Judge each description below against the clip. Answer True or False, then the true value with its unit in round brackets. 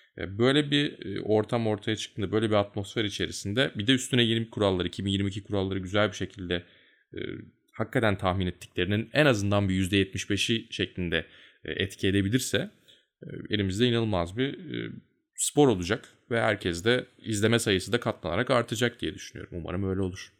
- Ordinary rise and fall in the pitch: True (3.5 semitones)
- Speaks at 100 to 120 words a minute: False (140 wpm)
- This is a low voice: True (105 Hz)